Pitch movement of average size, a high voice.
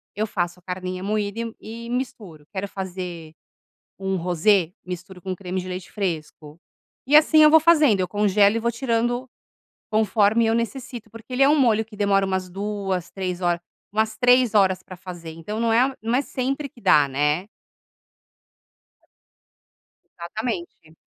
Yes: average, 4.2 semitones; high, 200 Hz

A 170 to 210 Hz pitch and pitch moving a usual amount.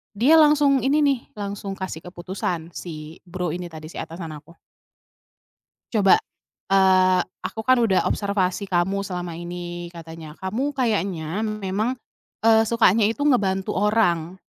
Yes: high, 190 Hz; average, 3.7 semitones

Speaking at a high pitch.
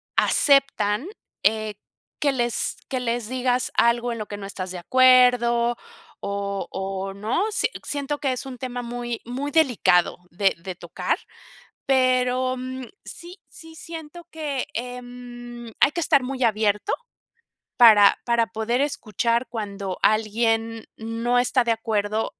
Yes: high, 240 Hz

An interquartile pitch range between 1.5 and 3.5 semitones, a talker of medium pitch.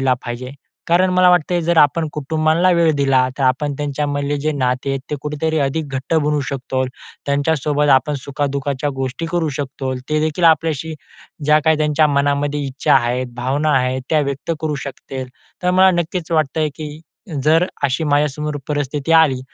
Yes: narrow, 2.6 semitones; medium, 145 Hz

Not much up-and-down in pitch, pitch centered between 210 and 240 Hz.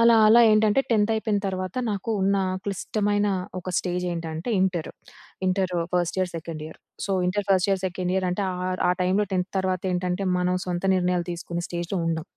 No: narrow, 2.2 semitones; medium, 185 Hz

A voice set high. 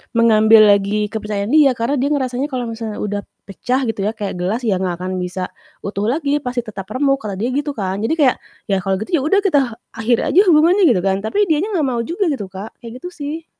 Yes: high, 230 Hz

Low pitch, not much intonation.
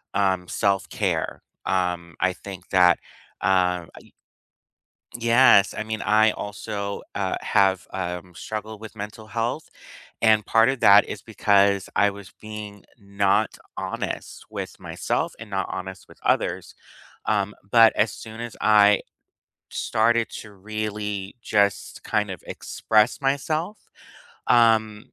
Yes: low, 105 Hz; narrow, 2.1 semitones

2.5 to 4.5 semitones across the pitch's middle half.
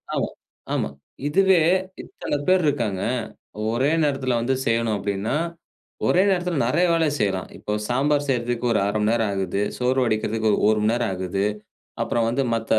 No: average, 5.0 semitones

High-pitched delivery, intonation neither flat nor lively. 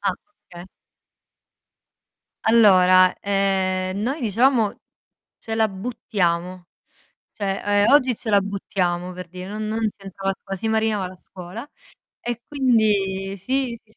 Yes: high, 200 Hz; average, 3.1 semitones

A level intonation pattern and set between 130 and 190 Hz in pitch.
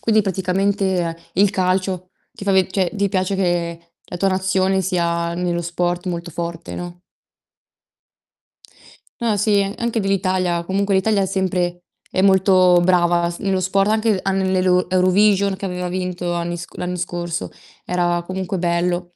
Yes: narrow, 1.7 semitones; medium, 185 Hz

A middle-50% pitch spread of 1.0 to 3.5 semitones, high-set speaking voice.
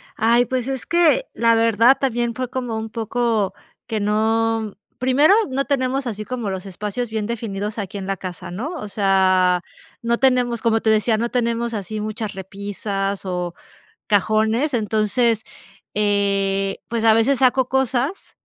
Yes: average, 3.2 semitones; high, 225 Hz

